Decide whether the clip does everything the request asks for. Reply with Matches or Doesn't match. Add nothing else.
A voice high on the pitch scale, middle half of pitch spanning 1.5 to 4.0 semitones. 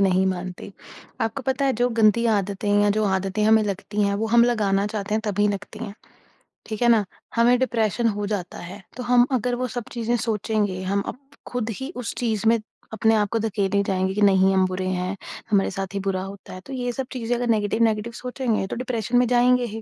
Matches